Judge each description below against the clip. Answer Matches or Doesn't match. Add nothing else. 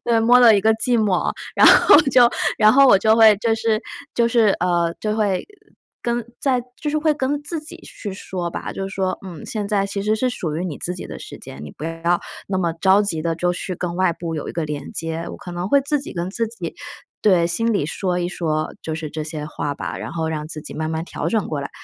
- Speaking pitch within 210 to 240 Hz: Doesn't match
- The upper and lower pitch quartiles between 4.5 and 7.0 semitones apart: Matches